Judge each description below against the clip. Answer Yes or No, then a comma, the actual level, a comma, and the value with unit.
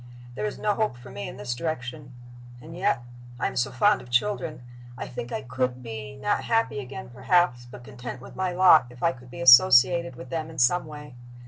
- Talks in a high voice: No, low, 130 Hz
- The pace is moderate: No, fast, 215 wpm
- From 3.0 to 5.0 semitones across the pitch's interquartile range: No, wide, 5.6 semitones